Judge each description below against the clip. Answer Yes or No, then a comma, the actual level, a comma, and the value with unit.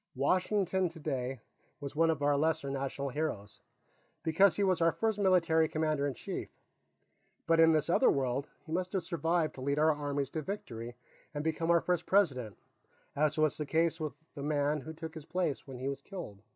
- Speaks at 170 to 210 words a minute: Yes, average, 190 wpm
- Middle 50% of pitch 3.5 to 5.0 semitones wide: No, average, 3.0 semitones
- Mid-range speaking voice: Yes, medium, 155 Hz